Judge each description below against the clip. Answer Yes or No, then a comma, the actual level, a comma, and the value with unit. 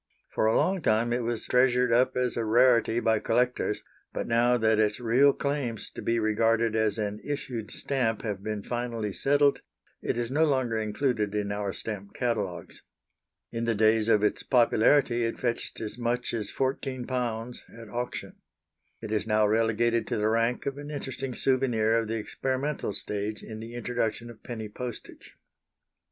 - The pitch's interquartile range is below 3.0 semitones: Yes, narrow, 2.4 semitones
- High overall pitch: No, low, 115 Hz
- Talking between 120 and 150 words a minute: No, average, 170 wpm